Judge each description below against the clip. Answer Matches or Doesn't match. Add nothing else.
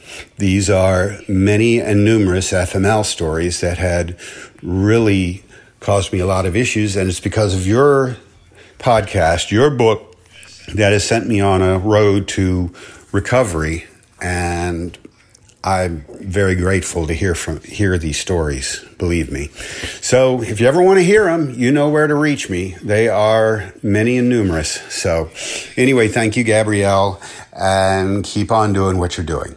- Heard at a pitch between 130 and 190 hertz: Doesn't match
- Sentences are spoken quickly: Doesn't match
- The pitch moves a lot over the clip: Doesn't match